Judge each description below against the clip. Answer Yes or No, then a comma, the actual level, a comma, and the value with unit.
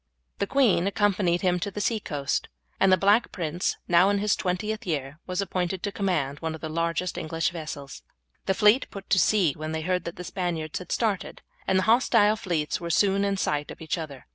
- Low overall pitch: No, medium, 180 Hz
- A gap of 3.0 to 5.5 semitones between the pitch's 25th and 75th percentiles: Yes, average, 3.7 semitones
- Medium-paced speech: No, fast, 220 wpm